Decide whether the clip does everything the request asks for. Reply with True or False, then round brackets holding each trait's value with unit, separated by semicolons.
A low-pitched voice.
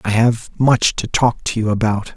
True (115 Hz)